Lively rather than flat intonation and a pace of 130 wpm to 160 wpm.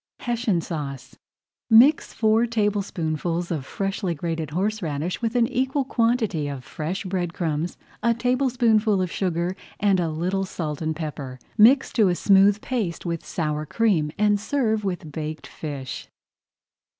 Yes: wide, 5.7 semitones; average, 140 wpm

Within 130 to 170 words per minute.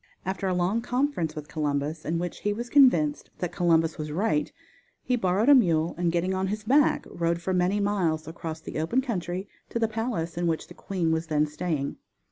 No: fast, 205 wpm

